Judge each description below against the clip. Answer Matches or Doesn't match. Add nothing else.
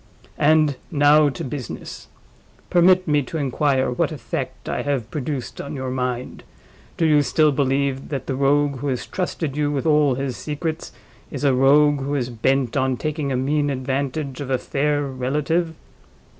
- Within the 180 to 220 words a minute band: Doesn't match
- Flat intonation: Matches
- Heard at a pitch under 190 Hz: Matches